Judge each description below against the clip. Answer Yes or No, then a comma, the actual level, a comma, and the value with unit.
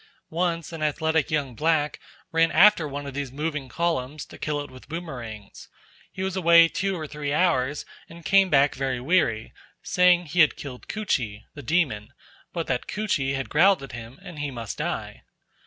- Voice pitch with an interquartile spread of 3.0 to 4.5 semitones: Yes, average, 4.1 semitones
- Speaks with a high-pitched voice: No, medium, 150 Hz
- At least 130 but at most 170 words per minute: No, average, 180 wpm